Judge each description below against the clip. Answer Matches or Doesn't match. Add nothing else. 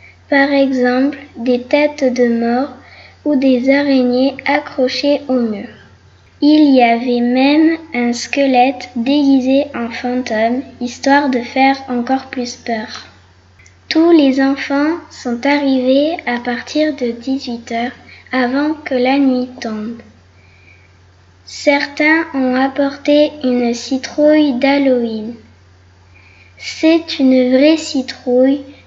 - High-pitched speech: Matches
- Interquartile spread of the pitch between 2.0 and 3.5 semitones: Matches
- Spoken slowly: Matches